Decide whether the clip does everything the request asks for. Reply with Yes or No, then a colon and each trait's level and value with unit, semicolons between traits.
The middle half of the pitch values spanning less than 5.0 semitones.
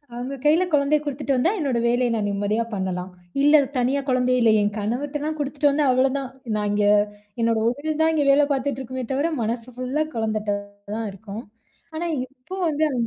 Yes: average, 4.4 semitones